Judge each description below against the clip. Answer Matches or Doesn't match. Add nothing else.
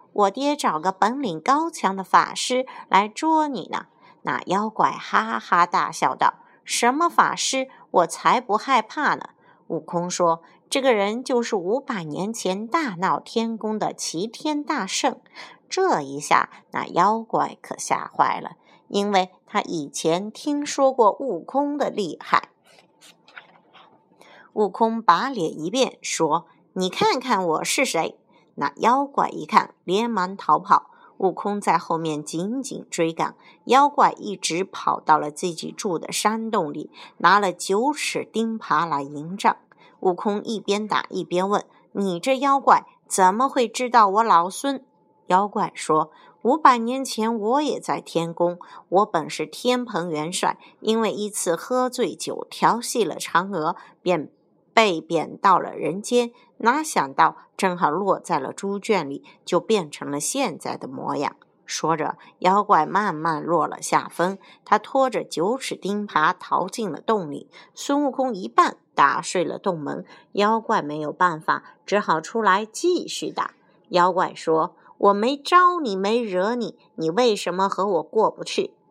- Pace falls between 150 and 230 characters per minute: Matches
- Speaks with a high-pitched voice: Matches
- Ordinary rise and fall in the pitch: Doesn't match